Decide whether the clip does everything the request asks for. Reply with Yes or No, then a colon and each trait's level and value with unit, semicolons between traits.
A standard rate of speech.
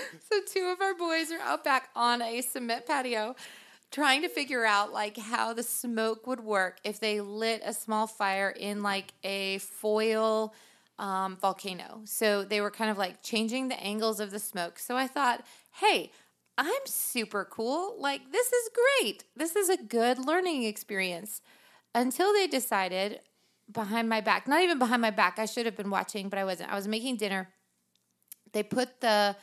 Yes: average, 180 wpm